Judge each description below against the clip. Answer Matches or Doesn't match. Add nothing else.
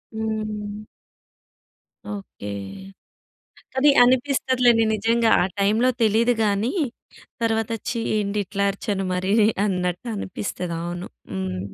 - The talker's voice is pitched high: Matches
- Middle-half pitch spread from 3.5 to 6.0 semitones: Doesn't match